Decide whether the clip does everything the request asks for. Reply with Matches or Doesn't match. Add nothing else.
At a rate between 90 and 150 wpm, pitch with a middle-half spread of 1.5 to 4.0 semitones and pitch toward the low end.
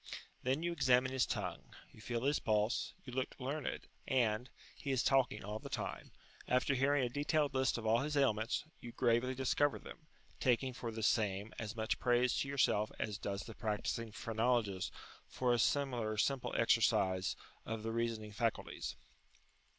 Doesn't match